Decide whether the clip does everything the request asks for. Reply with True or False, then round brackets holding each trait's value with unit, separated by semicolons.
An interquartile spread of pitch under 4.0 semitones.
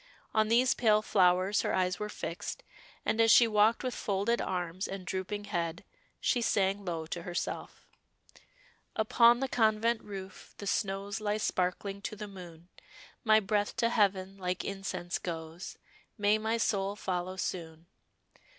True (2.9 semitones)